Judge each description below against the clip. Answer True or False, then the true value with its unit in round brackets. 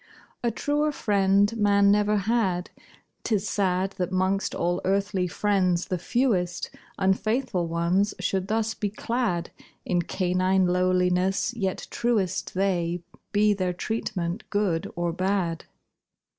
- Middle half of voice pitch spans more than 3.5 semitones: False (2.5 semitones)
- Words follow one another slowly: True (120 wpm)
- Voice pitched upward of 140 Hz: True (190 Hz)